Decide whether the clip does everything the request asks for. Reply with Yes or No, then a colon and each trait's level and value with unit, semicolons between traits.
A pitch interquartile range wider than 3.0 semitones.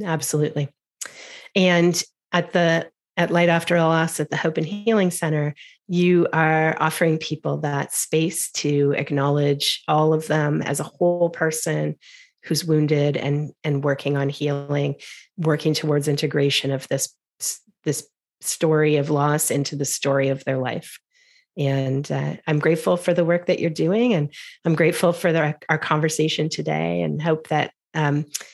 No: average, 2.7 semitones